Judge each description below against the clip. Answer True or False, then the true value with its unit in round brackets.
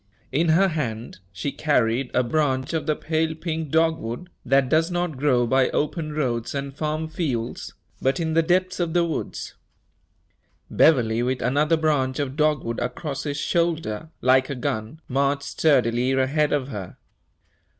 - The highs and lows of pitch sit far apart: False (3.9 semitones)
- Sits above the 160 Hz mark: False (145 Hz)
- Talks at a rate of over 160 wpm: False (155 wpm)